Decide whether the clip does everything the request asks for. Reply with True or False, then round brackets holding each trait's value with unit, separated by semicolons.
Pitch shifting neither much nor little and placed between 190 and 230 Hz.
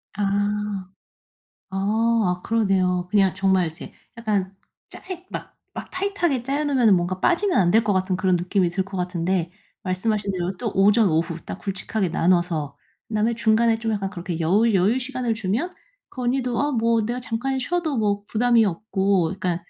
True (3.9 semitones; 205 Hz)